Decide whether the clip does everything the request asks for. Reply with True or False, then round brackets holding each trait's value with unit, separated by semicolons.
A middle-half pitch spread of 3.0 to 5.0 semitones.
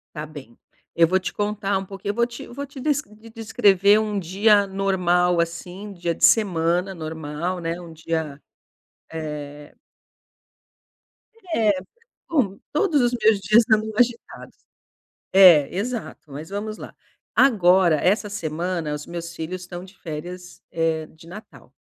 True (4.1 semitones)